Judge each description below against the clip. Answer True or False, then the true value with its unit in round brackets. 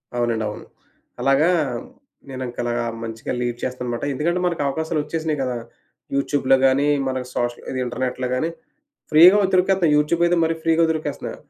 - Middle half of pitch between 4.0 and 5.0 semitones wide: True (4.5 semitones)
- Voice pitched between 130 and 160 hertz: True (140 Hz)